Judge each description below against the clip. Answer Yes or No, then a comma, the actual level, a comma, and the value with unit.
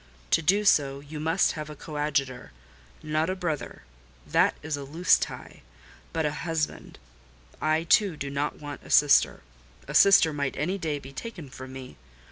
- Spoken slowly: No, average, 160 wpm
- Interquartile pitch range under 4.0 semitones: Yes, average, 2.9 semitones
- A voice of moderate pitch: Yes, medium, 150 Hz